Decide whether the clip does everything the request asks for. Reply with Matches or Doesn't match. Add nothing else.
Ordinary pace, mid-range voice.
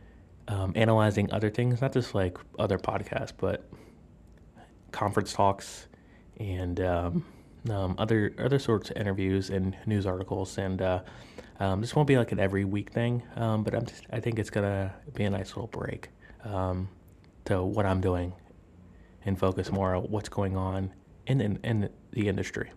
Doesn't match